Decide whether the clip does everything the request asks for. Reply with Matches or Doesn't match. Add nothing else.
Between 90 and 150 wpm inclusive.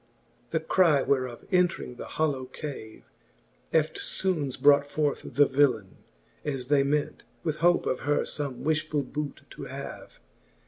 Matches